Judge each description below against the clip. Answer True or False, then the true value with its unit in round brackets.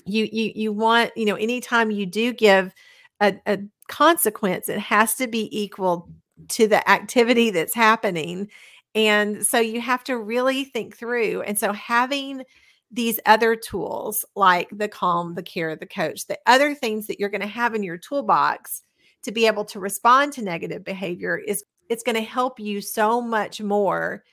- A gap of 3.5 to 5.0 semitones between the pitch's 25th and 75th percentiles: False (2.9 semitones)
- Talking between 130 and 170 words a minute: False (180 wpm)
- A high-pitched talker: True (215 Hz)